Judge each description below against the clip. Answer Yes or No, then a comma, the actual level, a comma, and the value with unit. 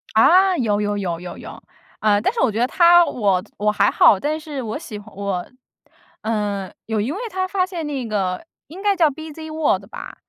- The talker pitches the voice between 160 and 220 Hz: No, high, 230 Hz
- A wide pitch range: Yes, wide, 7.8 semitones